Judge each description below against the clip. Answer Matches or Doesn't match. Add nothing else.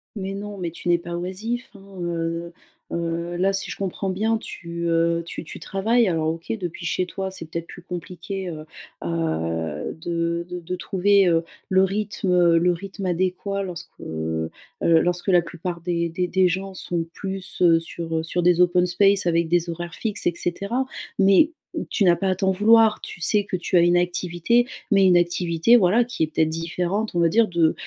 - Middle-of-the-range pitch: Matches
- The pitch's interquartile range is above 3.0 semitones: Doesn't match